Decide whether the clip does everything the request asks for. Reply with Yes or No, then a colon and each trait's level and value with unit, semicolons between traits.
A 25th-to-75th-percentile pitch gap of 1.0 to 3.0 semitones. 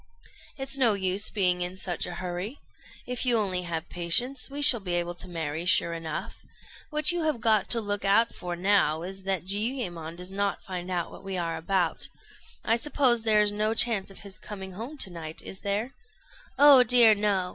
No: average, 4.4 semitones